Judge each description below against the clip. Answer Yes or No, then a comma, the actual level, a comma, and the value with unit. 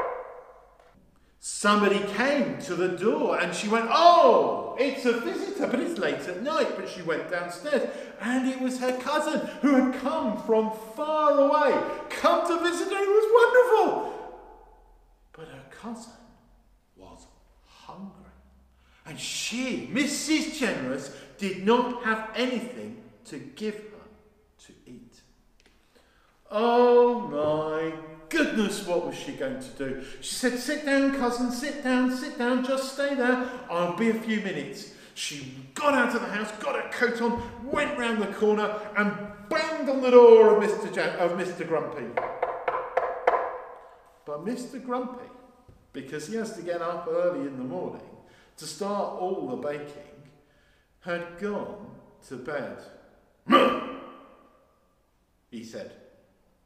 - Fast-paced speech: No, average, 140 wpm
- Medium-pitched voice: No, high, 225 Hz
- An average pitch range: No, wide, 7.1 semitones